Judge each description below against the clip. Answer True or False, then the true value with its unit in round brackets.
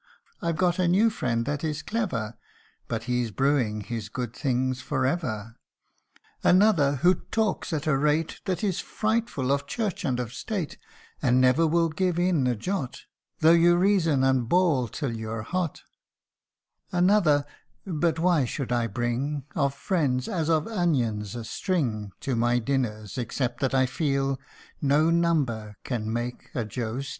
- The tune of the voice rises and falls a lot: True (5.9 semitones)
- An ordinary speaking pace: True (160 wpm)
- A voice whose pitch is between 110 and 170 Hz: True (140 Hz)